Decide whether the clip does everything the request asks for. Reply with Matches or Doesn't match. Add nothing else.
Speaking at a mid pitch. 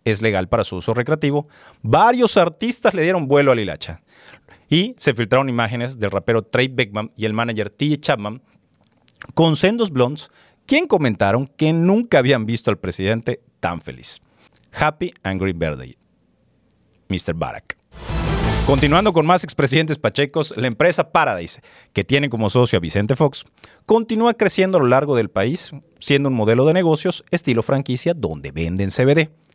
Doesn't match